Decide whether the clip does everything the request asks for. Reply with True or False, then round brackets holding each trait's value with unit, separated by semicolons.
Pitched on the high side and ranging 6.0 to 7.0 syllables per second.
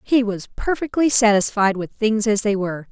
False (220 Hz; 5.1 syllables/s)